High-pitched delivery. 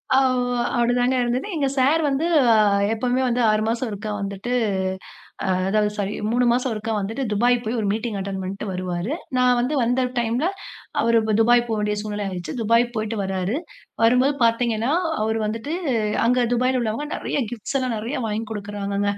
Yes: high, 230 Hz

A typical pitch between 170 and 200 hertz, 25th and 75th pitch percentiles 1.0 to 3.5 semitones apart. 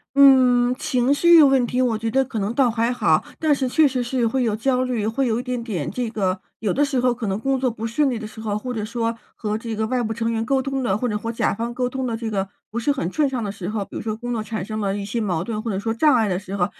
No: high, 230 Hz; average, 3.0 semitones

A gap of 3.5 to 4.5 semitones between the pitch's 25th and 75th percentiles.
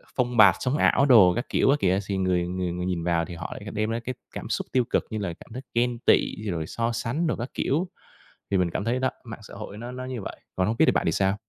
No: average, 4.9 semitones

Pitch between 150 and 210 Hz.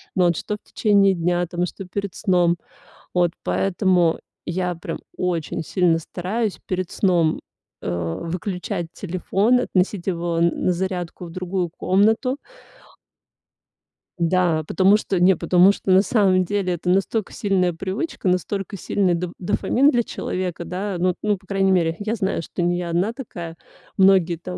Yes: medium, 185 Hz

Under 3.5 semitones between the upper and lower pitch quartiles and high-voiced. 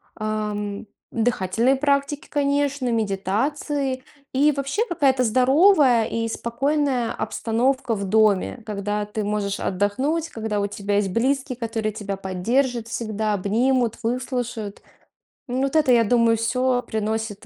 No: average, 4.0 semitones; high, 230 Hz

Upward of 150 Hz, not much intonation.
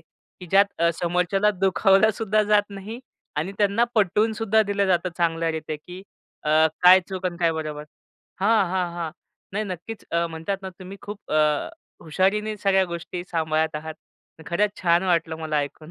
No: medium, 185 Hz; average, 3.6 semitones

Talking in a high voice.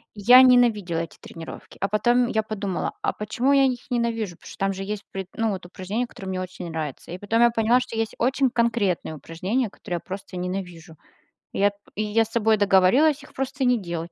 Yes: high, 210 Hz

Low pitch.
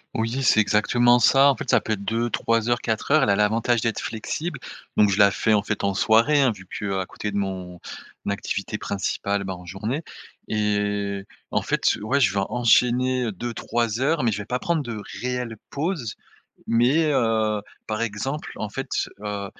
Yes: low, 110 Hz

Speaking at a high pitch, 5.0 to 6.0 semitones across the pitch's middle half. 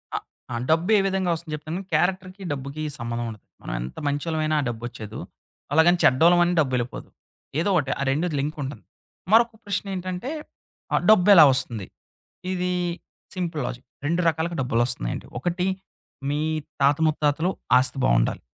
No: medium, 155 Hz; wide, 5.5 semitones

